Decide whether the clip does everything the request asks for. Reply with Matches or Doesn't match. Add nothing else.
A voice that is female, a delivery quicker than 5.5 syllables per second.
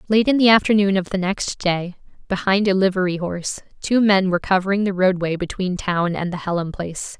Matches